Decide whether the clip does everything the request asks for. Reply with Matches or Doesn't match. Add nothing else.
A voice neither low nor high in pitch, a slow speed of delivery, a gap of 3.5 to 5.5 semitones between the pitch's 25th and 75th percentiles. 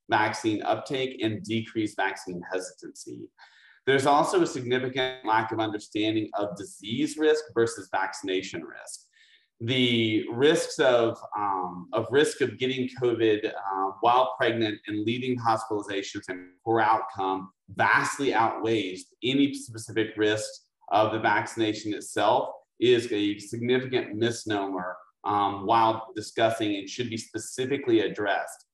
Doesn't match